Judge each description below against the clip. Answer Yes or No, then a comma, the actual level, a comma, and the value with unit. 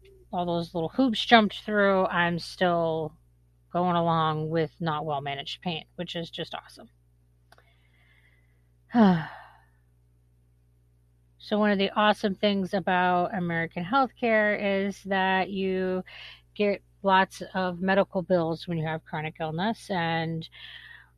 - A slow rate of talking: Yes, slow, 120 wpm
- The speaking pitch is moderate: Yes, medium, 170 Hz